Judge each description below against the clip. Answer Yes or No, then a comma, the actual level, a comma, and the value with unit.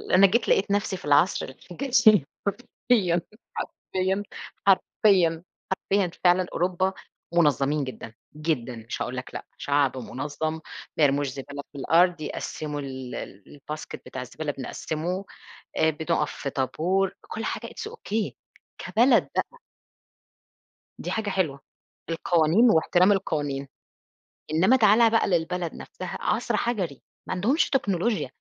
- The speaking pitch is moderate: Yes, medium, 170 Hz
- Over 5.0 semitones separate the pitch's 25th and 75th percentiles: Yes, wide, 5.4 semitones